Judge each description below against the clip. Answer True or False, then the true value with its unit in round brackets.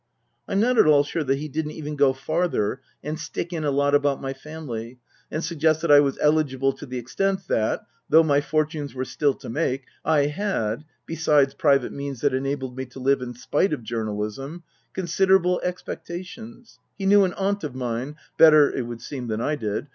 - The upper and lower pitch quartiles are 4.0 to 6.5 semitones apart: False (3.5 semitones)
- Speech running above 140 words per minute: True (195 wpm)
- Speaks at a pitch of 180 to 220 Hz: False (145 Hz)